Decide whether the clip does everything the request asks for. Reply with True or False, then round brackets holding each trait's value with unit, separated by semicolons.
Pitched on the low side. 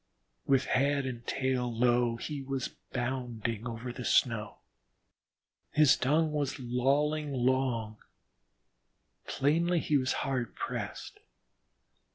True (130 Hz)